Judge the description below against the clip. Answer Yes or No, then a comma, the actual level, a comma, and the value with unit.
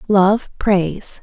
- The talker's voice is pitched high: Yes, high, 195 Hz